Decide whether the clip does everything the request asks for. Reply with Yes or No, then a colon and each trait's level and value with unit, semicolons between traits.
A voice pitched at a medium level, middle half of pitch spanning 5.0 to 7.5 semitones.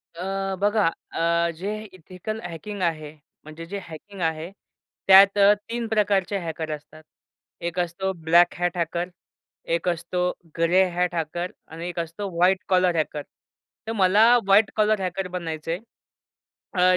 No: medium, 180 Hz; average, 2.8 semitones